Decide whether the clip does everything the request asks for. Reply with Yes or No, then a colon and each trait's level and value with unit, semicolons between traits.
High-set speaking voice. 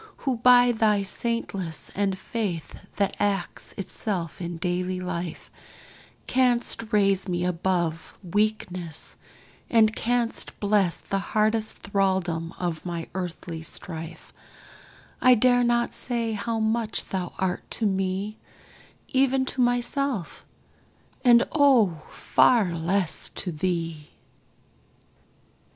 Yes: high, 195 Hz